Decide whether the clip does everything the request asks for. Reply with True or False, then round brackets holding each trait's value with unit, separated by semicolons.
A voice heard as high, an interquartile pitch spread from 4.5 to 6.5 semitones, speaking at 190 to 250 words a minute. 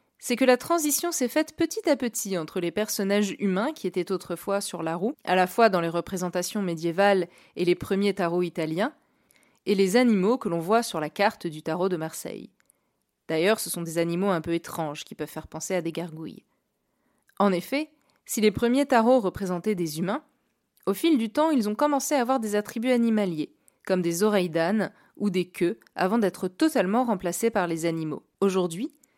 True (200 Hz; 5.3 semitones; 195 wpm)